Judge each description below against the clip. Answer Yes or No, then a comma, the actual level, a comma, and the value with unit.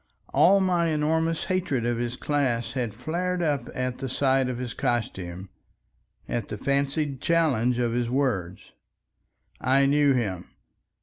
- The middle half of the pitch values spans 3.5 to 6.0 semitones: Yes, average, 4.2 semitones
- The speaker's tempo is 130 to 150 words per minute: Yes, average, 140 wpm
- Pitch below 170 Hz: Yes, low, 135 Hz